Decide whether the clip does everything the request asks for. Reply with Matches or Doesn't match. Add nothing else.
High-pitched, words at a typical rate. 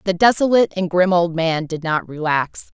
Doesn't match